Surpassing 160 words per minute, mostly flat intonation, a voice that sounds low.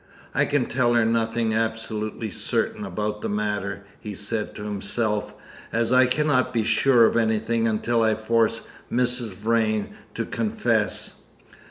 No: average, 145 wpm; narrow, 1.7 semitones; low, 115 Hz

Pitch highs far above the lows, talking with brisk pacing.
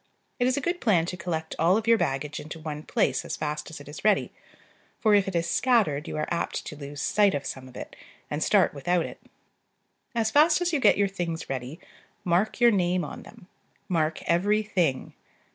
Yes: wide, 5.8 semitones; fast, 210 wpm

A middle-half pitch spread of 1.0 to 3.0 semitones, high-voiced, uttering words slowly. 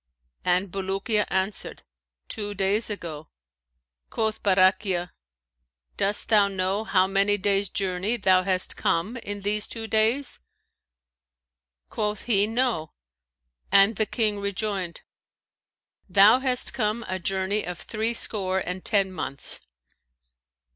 Yes: narrow, 2.4 semitones; high, 200 Hz; slow, 115 wpm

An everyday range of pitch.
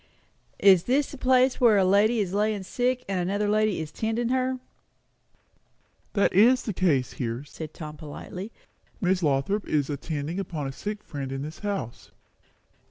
No: wide, 6.1 semitones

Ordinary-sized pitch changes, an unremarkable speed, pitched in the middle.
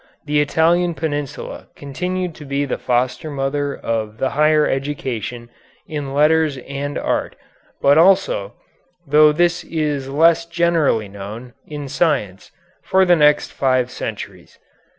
No: average, 3.4 semitones; slow, 130 wpm; medium, 145 Hz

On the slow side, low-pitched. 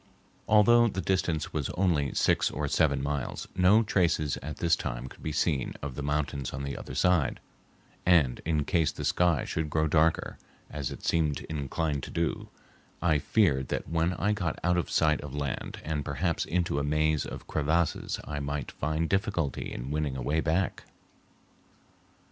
No: average, 175 wpm; very low, 75 Hz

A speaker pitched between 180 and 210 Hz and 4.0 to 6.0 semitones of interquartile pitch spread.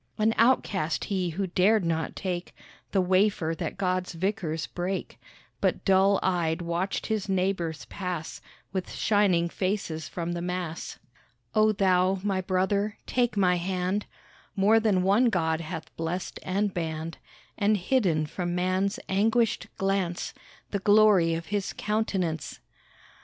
No: medium, 185 Hz; average, 2.8 semitones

